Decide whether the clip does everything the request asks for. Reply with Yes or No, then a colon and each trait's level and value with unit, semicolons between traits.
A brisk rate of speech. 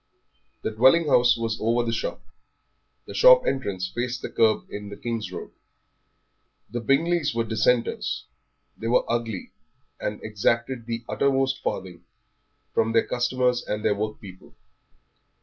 No: slow, 135 wpm